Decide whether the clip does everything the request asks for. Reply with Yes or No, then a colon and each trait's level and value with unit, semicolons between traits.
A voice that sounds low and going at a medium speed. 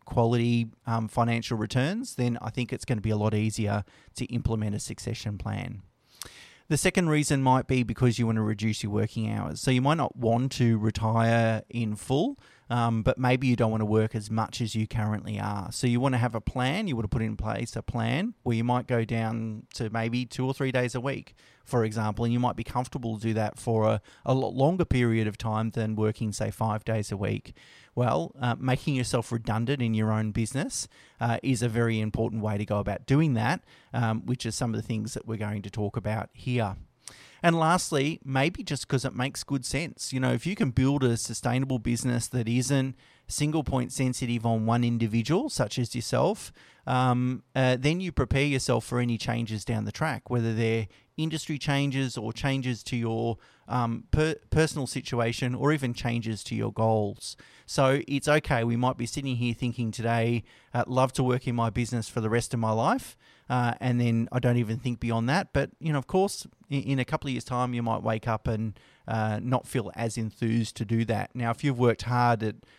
No: low, 120 Hz; fast, 215 wpm